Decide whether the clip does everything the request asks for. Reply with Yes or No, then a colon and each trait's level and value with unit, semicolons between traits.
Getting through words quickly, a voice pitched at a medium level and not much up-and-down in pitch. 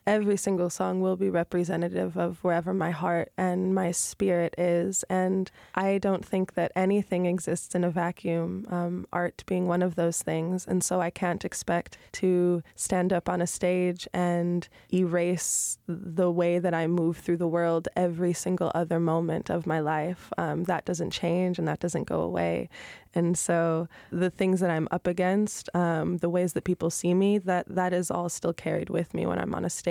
No: average, 195 wpm; medium, 175 Hz; narrow, 1.3 semitones